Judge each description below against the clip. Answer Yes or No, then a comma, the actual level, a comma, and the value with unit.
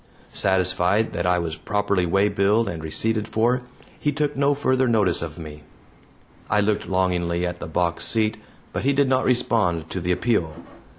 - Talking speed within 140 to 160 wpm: No, average, 170 wpm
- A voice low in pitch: Yes, low, 100 Hz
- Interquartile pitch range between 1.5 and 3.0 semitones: No, average, 4.7 semitones